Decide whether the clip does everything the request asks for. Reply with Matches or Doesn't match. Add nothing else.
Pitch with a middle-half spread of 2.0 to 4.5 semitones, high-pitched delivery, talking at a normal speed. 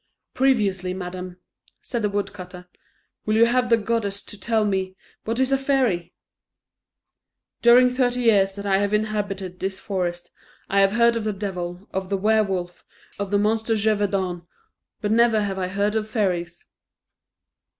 Matches